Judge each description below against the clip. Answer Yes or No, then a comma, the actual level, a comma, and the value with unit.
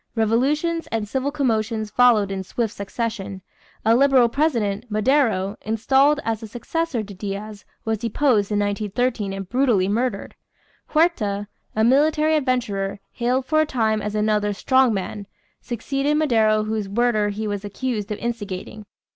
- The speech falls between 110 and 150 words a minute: Yes, average, 145 wpm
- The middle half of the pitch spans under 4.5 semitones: Yes, average, 3.9 semitones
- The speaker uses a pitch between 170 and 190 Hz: No, high, 225 Hz